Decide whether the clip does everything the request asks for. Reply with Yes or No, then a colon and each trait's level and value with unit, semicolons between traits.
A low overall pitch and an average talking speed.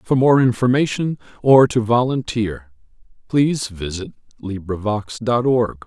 No: low, 115 Hz; slow, 115 wpm